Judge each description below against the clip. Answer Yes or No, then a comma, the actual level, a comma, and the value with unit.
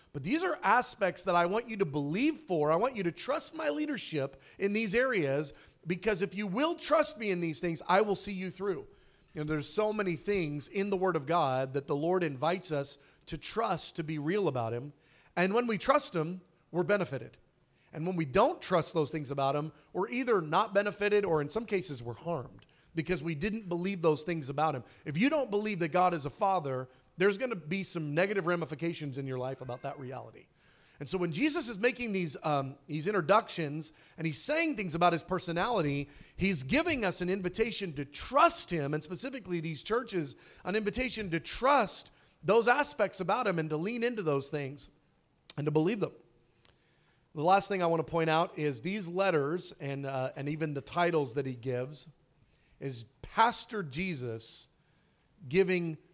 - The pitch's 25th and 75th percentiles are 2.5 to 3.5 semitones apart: No, average, 5.0 semitones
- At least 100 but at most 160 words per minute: No, average, 200 wpm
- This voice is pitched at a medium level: Yes, medium, 175 Hz